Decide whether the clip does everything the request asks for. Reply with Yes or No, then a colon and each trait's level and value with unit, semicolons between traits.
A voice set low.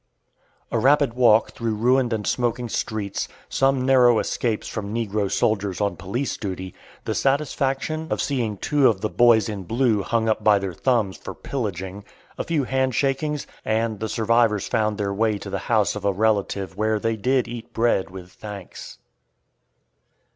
Yes: low, 110 Hz